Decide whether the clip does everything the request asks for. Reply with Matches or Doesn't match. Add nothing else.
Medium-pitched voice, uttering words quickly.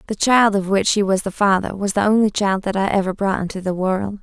Doesn't match